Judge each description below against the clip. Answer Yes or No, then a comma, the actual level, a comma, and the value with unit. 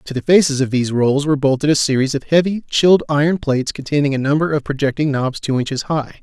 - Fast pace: Yes, fast, 230 wpm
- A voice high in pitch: No, medium, 145 Hz